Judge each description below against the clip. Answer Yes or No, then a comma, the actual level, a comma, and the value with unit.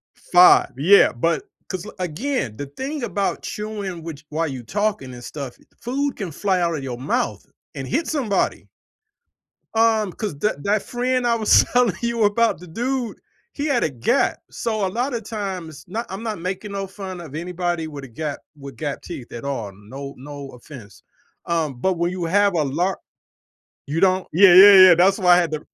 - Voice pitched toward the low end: No, medium, 180 Hz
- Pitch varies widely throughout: Yes, wide, 6.4 semitones